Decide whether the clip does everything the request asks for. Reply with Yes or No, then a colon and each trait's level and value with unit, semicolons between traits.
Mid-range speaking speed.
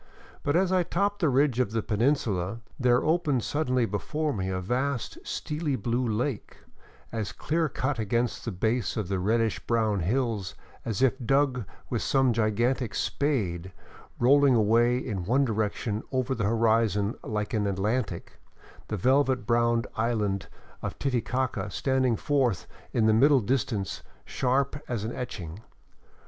Yes: average, 145 wpm